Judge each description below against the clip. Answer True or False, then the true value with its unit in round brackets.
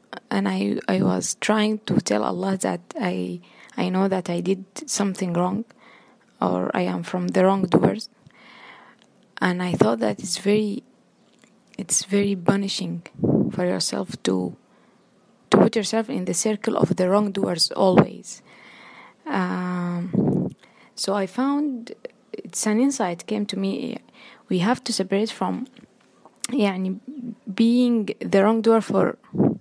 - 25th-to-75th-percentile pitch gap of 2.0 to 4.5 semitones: True (3.7 semitones)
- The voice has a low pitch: False (205 Hz)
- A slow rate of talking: True (130 wpm)